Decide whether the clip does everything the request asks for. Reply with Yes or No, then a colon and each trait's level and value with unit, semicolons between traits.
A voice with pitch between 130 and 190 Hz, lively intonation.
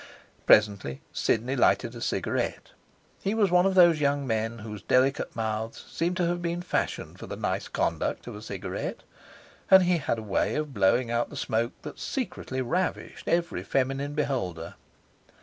Yes: low, 135 Hz; wide, 7.3 semitones